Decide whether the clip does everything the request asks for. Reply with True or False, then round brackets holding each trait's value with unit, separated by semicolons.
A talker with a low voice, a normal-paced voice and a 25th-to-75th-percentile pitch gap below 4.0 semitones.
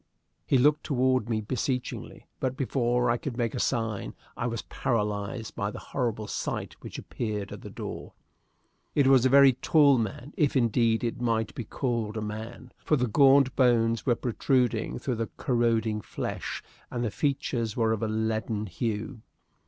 True (120 Hz; 170 wpm; 2.7 semitones)